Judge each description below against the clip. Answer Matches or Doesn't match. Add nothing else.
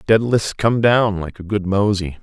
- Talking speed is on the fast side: Doesn't match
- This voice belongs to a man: Matches